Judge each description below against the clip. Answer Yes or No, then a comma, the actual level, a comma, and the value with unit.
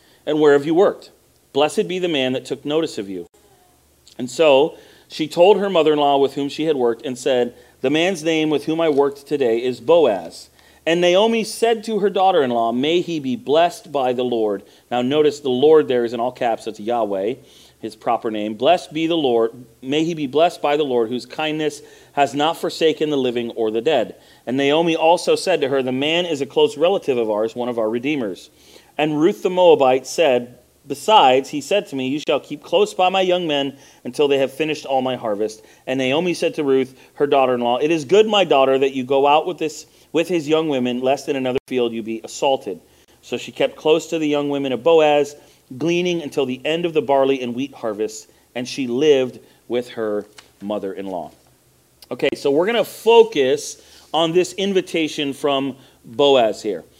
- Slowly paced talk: No, fast, 205 wpm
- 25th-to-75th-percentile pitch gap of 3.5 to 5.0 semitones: Yes, average, 4.7 semitones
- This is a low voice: No, medium, 145 Hz